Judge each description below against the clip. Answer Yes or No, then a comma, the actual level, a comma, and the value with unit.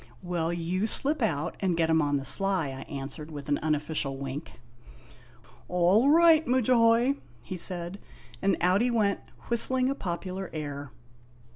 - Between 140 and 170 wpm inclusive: Yes, average, 150 wpm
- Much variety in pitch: Yes, wide, 7.2 semitones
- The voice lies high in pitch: No, medium, 180 Hz